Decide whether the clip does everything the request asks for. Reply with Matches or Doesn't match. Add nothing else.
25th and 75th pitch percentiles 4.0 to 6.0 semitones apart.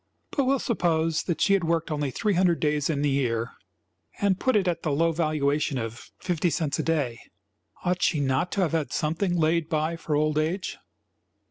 Doesn't match